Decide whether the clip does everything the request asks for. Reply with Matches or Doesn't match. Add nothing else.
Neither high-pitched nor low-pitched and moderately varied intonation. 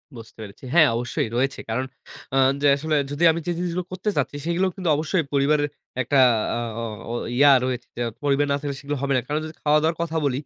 Matches